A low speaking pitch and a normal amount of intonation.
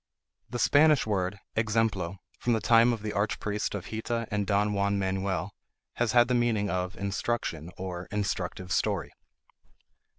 Yes: low, 105 Hz; average, 3.0 semitones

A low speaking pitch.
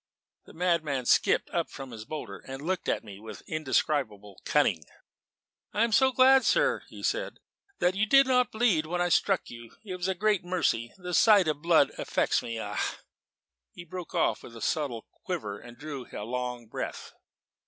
No: medium, 155 Hz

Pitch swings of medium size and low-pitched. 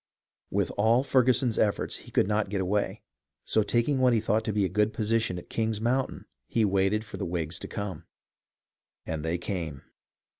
Yes: average, 3.2 semitones; low, 105 Hz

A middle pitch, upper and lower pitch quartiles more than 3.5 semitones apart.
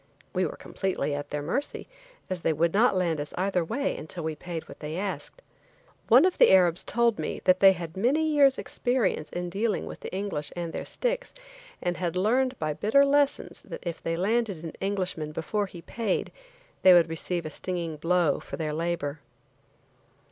Yes: medium, 180 Hz; average, 5.1 semitones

